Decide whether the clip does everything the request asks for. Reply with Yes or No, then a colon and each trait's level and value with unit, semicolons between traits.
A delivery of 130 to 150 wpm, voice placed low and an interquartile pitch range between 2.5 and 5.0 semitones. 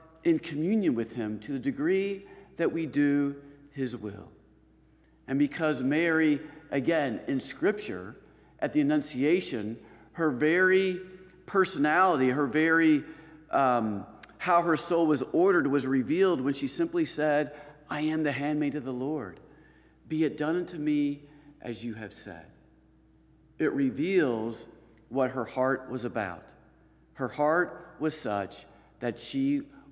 No: slow, 135 wpm; medium, 150 Hz; average, 4.7 semitones